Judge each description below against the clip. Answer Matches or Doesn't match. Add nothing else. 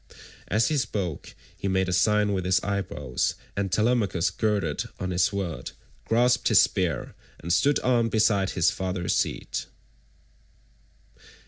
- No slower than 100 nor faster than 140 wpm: Matches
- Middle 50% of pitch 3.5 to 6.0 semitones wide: Doesn't match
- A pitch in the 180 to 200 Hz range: Doesn't match